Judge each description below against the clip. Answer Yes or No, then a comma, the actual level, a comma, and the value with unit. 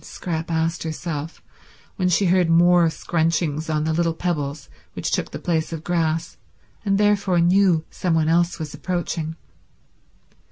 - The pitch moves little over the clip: Yes, narrow, 1.8 semitones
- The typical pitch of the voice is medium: Yes, medium, 165 Hz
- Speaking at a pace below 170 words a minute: Yes, average, 150 wpm